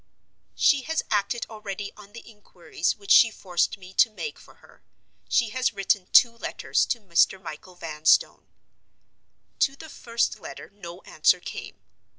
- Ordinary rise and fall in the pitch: Yes, average, 4.1 semitones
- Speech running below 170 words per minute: Yes, average, 155 wpm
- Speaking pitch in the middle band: No, high, 205 Hz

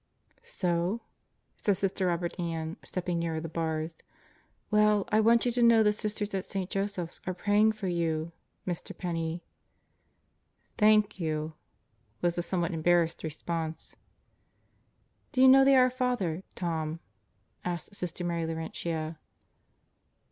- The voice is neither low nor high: Yes, medium, 175 Hz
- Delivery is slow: Yes, slow, 130 wpm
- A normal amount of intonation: Yes, average, 4.2 semitones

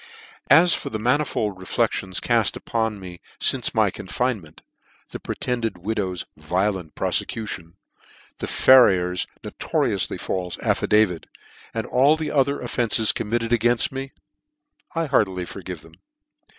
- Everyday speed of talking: No, slow, 120 wpm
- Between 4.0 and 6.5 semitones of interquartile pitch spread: Yes, average, 5.2 semitones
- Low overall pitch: Yes, low, 110 Hz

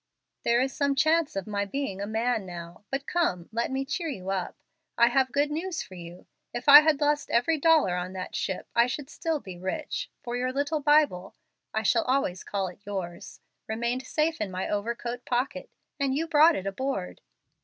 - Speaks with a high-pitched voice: Yes, high, 245 Hz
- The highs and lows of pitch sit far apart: Yes, wide, 6.9 semitones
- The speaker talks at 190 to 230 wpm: Yes, average, 195 wpm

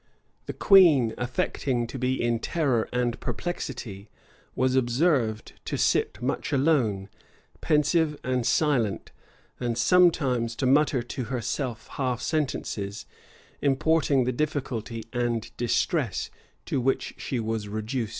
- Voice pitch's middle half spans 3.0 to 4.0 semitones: Yes, average, 3.6 semitones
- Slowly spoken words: Yes, slow, 120 wpm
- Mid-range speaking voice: No, low, 125 Hz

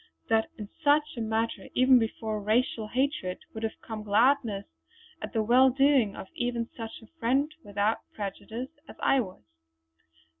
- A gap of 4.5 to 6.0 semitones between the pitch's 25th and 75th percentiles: No, average, 3.2 semitones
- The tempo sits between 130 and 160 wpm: Yes, average, 155 wpm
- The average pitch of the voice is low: No, high, 230 Hz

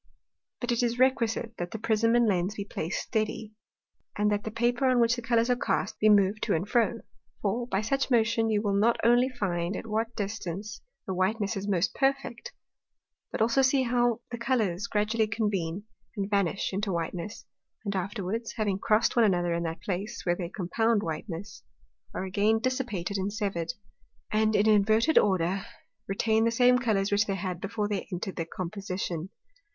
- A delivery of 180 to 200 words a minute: Yes, average, 185 wpm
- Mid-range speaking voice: No, high, 210 Hz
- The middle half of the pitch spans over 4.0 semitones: No, average, 3.2 semitones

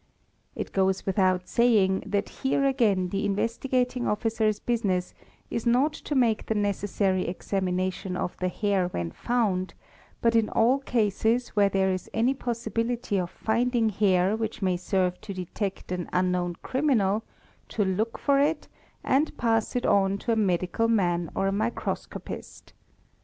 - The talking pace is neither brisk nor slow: Yes, average, 150 wpm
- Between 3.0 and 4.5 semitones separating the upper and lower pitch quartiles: Yes, average, 3.9 semitones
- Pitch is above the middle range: Yes, high, 205 Hz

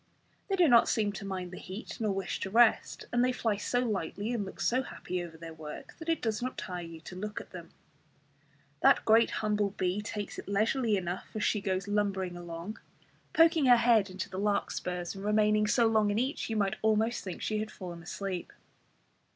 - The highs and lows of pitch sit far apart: No, average, 3.3 semitones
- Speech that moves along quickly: Yes, fast, 210 wpm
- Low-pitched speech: No, high, 210 Hz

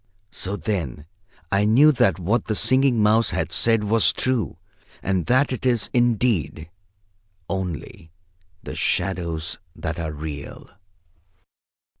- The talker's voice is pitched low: Yes, low, 100 Hz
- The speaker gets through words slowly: Yes, slow, 120 wpm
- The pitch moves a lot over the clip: Yes, wide, 5.9 semitones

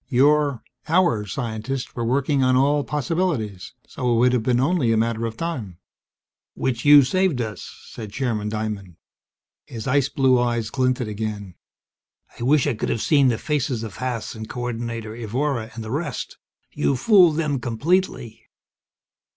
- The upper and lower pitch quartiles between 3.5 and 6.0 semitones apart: Yes, average, 4.1 semitones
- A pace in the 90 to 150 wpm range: No, average, 165 wpm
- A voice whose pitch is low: Yes, low, 125 Hz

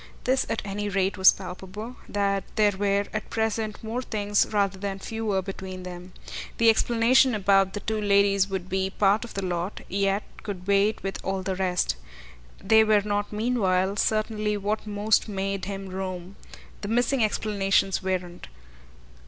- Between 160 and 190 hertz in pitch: No, high, 200 Hz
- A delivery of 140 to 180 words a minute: Yes, average, 160 wpm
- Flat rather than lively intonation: Yes, narrow, 2.0 semitones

